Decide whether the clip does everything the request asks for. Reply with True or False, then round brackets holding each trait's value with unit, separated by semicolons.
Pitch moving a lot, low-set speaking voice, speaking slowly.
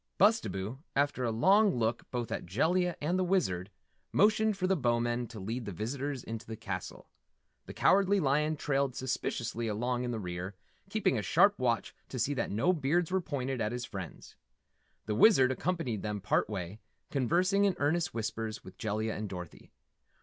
False (7.9 semitones; 125 Hz; 175 wpm)